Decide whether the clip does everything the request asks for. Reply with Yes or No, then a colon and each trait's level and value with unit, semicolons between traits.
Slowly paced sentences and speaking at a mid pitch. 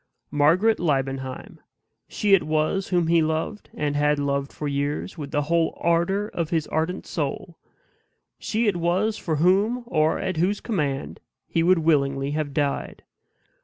No: average, 155 wpm; medium, 160 Hz